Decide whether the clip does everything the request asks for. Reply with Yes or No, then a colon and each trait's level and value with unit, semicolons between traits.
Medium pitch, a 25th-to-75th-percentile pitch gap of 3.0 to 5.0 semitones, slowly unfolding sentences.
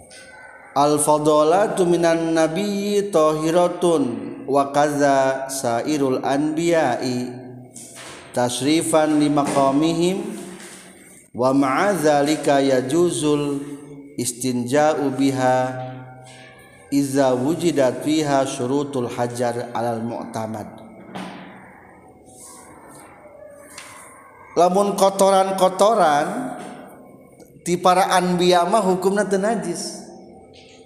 No: medium, 150 Hz; wide, 5.4 semitones; slow, 60 wpm